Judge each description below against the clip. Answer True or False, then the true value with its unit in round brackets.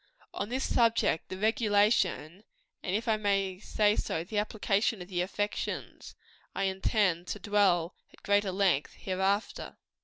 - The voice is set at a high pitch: True (200 Hz)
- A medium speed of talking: True (150 wpm)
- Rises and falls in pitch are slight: True (2.2 semitones)